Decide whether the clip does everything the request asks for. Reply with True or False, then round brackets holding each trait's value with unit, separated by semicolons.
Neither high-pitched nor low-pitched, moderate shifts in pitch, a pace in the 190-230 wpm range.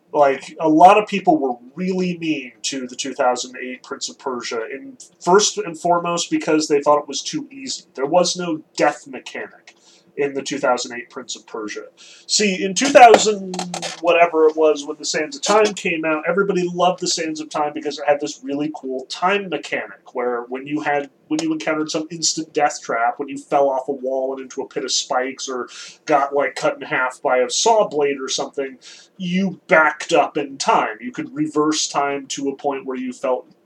True (155 Hz; 4.8 semitones; 205 wpm)